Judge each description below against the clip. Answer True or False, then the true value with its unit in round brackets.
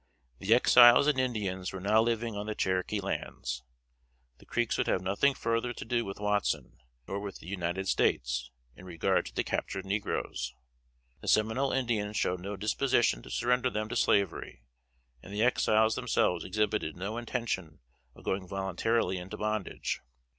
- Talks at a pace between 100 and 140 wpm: False (160 wpm)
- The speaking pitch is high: False (105 Hz)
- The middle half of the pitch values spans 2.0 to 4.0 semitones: True (3.6 semitones)